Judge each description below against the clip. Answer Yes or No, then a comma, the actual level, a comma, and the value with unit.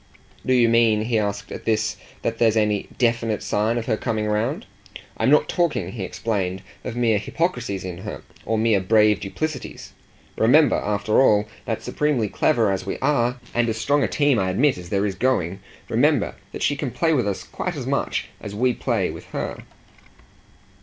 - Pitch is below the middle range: Yes, low, 115 Hz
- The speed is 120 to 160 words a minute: No, average, 185 wpm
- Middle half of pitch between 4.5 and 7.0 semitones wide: No, average, 3.5 semitones